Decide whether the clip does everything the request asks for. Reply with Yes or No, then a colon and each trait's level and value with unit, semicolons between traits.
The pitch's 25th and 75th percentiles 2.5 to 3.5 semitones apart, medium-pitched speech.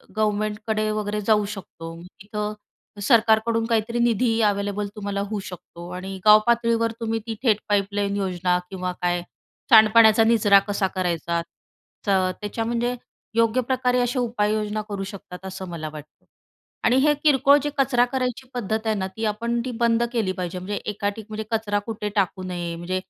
No: average, 3.0 semitones; high, 210 Hz